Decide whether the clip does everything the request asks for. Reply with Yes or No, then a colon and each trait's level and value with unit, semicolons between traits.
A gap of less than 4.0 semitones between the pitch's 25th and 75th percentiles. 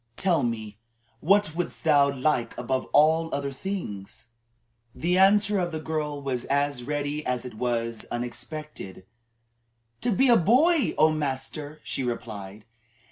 No: average, 5.2 semitones